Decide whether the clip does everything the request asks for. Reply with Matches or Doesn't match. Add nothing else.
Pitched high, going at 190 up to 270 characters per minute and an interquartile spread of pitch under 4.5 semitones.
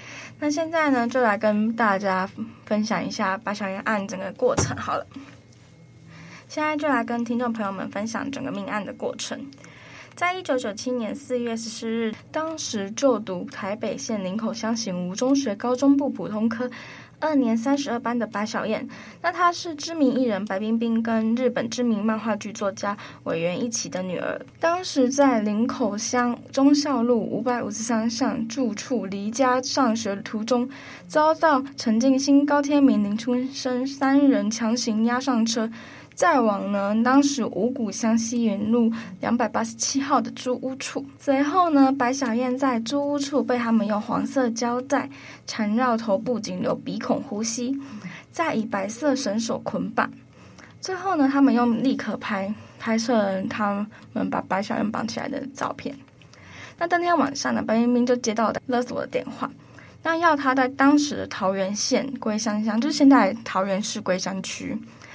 Matches